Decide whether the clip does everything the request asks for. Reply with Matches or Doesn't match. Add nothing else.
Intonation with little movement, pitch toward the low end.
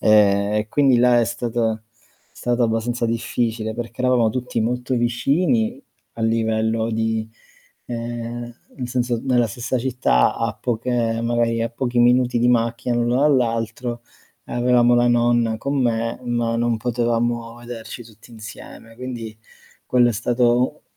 Matches